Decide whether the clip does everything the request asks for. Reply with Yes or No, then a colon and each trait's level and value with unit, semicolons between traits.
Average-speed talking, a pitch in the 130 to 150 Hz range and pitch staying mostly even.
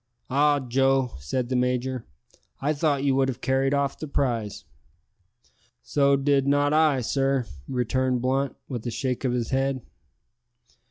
Yes: average, 150 wpm; low, 135 Hz; narrow, 1.7 semitones